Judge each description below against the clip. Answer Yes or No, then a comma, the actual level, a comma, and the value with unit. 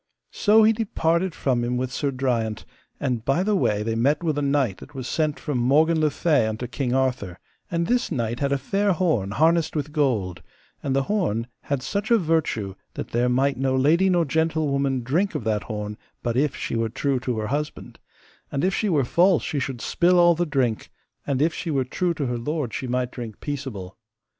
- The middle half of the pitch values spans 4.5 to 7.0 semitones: Yes, average, 5.1 semitones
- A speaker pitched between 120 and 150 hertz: Yes, medium, 140 Hz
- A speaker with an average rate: No, fast, 210 wpm